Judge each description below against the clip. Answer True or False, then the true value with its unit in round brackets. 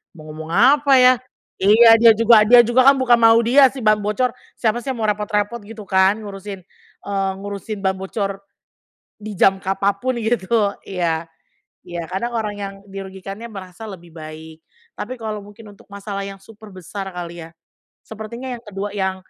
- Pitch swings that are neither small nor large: True (3.0 semitones)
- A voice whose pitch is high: True (205 Hz)